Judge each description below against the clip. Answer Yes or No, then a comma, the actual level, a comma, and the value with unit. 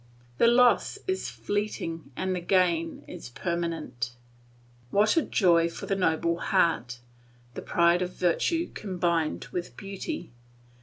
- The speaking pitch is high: No, medium, 175 Hz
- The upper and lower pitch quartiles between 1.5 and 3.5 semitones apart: Yes, average, 3.0 semitones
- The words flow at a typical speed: No, slow, 120 wpm